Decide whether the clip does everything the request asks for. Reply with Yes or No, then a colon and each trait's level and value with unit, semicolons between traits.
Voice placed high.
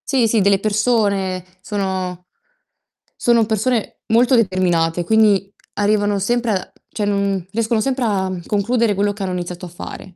Yes: high, 205 Hz